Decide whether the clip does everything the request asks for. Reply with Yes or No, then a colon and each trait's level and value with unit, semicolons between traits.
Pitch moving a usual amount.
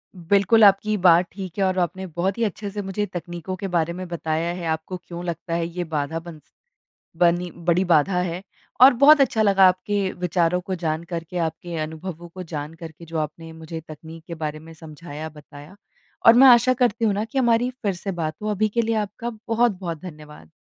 Yes: average, 3.6 semitones